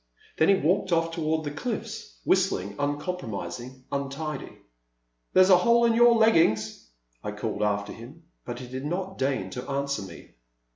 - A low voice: No, medium, 145 Hz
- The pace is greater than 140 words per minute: Yes, average, 175 wpm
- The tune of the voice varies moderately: No, wide, 7.1 semitones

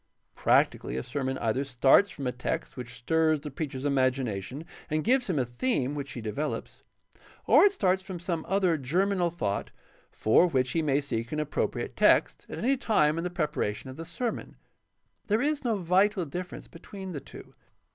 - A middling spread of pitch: No, wide, 6.0 semitones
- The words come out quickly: No, average, 185 wpm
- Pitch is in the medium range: Yes, medium, 155 Hz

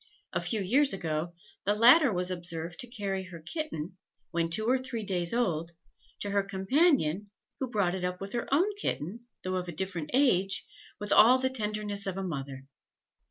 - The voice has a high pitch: Yes, high, 195 Hz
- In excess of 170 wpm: Yes, average, 185 wpm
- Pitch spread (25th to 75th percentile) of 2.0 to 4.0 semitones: No, average, 5.2 semitones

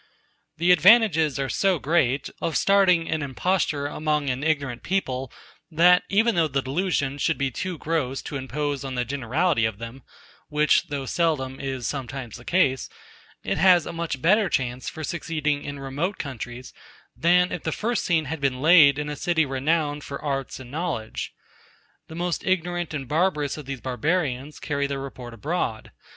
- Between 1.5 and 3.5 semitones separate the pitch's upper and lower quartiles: No, average, 4.2 semitones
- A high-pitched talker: No, medium, 150 Hz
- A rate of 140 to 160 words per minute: No, average, 170 wpm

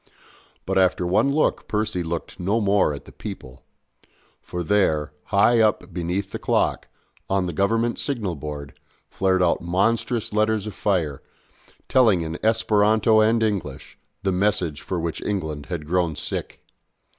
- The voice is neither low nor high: No, very low, 95 Hz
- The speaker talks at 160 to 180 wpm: No, average, 145 wpm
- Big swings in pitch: No, average, 4.2 semitones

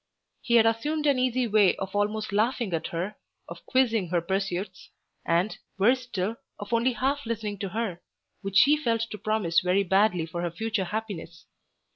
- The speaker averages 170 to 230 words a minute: Yes, average, 175 wpm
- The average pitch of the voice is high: Yes, high, 210 Hz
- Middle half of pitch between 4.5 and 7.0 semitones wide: No, average, 3.7 semitones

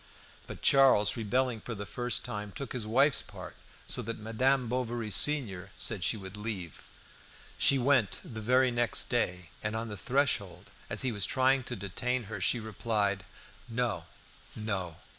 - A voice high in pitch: No, low, 115 Hz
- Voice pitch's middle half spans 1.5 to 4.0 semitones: Yes, average, 3.7 semitones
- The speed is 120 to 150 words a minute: No, average, 160 wpm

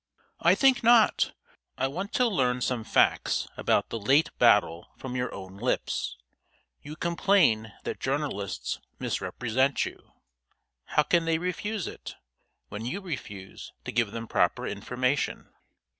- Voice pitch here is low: Yes, low, 130 Hz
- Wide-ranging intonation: Yes, wide, 7.4 semitones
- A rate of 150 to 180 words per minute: No, slow, 135 wpm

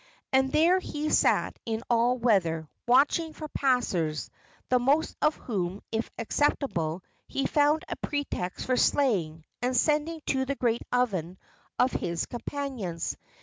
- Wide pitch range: Yes, wide, 7.3 semitones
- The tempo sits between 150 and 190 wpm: No, average, 140 wpm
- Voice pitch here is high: Yes, very high, 250 Hz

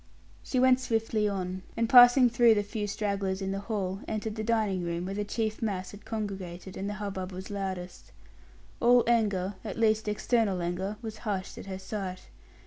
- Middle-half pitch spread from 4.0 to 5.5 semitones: No, average, 2.8 semitones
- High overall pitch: Yes, high, 205 Hz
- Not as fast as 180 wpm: No, average, 185 wpm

